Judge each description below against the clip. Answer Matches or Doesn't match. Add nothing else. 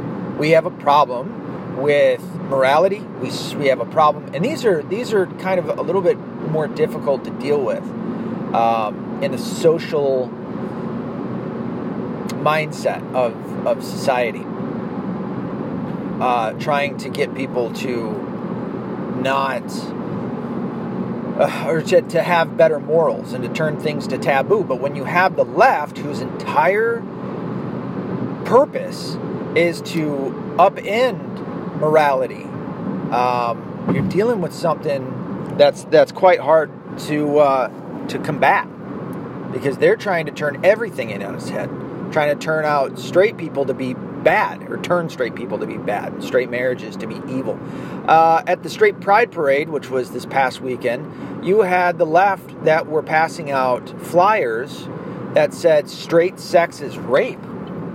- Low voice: Doesn't match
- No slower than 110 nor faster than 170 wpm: Matches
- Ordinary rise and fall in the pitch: Matches